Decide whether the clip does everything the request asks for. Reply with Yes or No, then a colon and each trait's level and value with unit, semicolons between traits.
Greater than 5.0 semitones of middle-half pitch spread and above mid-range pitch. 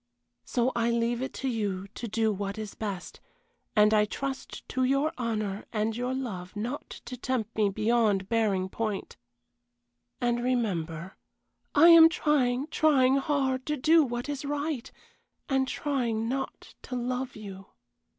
No: average, 3.9 semitones; high, 240 Hz